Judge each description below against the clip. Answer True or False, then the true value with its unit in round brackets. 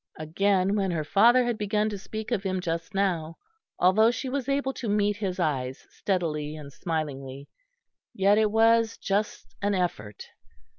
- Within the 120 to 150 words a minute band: False (160 wpm)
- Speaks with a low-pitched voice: False (195 Hz)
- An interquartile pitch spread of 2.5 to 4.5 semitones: False (5.1 semitones)